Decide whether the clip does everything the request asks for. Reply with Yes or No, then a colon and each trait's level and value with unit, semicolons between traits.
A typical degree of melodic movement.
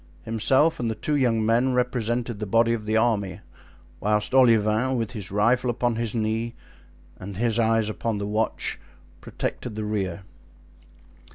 No: narrow, 2.2 semitones